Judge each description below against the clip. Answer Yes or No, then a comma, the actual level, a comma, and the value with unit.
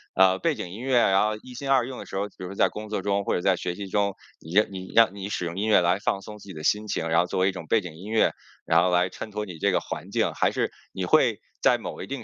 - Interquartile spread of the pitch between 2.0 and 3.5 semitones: Yes, average, 2.8 semitones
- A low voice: Yes, low, 100 Hz